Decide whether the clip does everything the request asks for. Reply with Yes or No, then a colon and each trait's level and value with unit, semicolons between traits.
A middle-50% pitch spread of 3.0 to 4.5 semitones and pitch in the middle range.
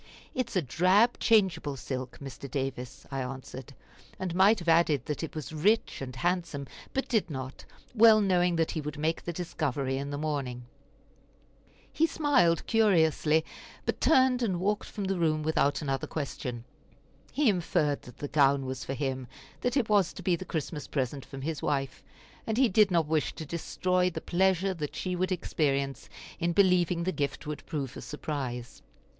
No: average, 5.1 semitones; medium, 160 Hz